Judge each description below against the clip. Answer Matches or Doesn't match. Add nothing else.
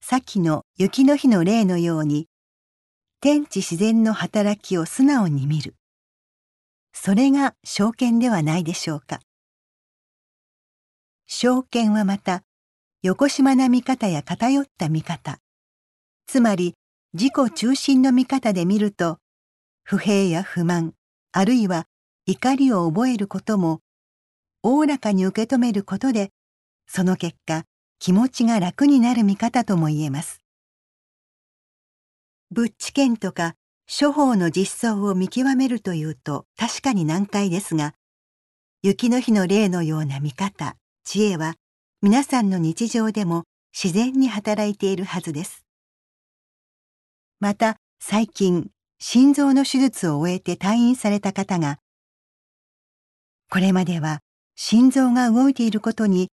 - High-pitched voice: Matches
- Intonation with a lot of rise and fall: Matches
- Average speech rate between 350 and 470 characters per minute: Doesn't match